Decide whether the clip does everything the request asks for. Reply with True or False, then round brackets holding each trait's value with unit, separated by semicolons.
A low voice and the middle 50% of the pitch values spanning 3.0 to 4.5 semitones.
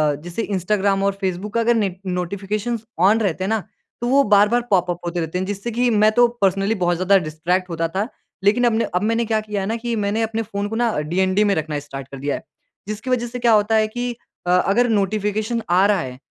False (205 Hz; 3.6 semitones)